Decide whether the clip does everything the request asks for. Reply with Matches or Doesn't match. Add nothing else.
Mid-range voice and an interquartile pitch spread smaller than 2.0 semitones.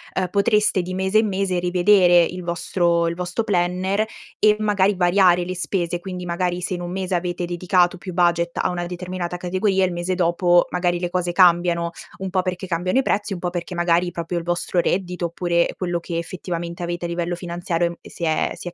Matches